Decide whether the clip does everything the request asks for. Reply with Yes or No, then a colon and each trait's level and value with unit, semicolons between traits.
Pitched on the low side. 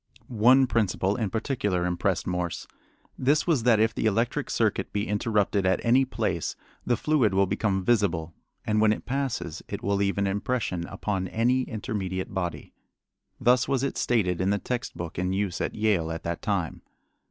Yes: low, 105 Hz